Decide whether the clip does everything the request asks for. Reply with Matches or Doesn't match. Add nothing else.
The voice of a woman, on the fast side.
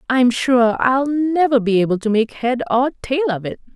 Matches